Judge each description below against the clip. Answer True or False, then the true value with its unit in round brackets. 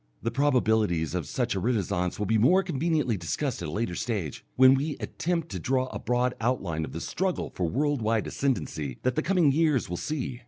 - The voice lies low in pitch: True (120 Hz)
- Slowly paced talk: False (205 wpm)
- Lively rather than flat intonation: True (7.4 semitones)